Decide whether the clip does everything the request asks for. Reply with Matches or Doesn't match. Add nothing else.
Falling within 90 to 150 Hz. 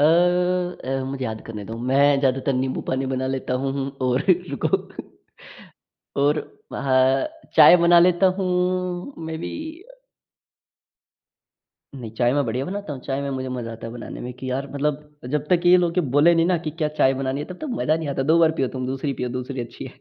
Matches